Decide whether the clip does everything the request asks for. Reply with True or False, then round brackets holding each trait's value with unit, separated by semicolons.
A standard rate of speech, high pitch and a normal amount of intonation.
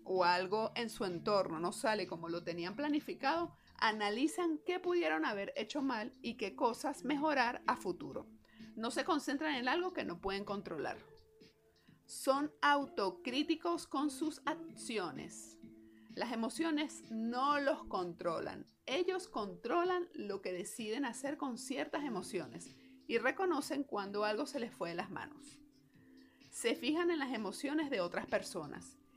False (140 wpm; 270 Hz; 6.8 semitones)